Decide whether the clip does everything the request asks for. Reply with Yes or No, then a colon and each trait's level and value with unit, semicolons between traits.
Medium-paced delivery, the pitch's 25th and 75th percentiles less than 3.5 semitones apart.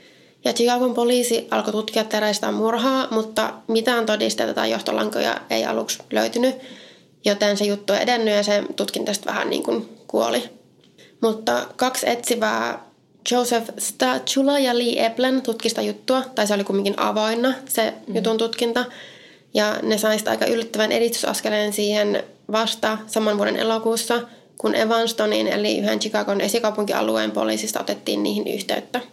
Yes: average, 140 wpm; narrow, 2.4 semitones